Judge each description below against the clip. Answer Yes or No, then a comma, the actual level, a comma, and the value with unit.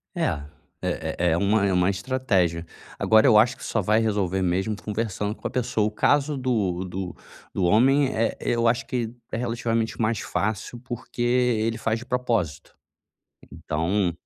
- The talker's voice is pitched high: No, low, 110 Hz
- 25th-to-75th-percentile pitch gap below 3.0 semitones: No, average, 4.0 semitones